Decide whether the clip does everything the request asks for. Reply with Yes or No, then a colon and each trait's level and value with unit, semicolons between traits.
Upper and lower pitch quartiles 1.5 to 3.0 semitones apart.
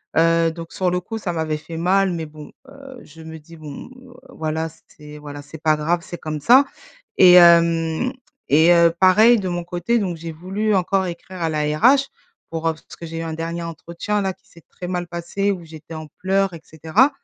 Yes: average, 2.7 semitones